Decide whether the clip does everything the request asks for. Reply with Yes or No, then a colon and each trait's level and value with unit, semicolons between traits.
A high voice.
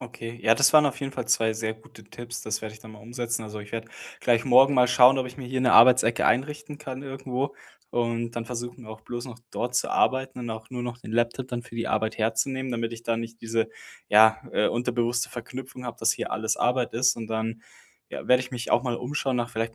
No: low, 120 Hz